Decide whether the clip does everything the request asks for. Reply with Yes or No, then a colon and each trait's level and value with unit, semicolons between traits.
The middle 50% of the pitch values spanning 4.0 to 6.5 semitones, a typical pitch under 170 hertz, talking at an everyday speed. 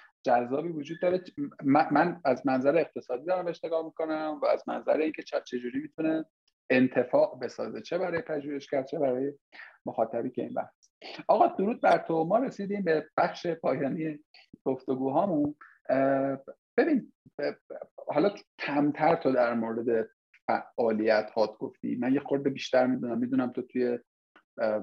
Yes: average, 4.5 semitones; medium, 140 Hz; average, 140 wpm